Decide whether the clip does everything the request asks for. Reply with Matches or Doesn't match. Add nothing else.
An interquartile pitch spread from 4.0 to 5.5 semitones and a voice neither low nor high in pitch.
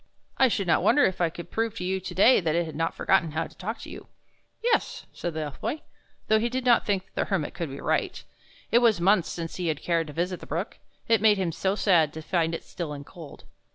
Matches